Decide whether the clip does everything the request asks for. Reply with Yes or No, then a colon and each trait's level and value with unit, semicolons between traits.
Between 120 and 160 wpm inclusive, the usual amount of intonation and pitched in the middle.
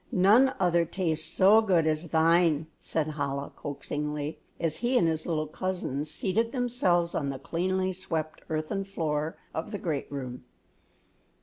Yes: average, 145 wpm; average, 3.6 semitones; medium, 165 Hz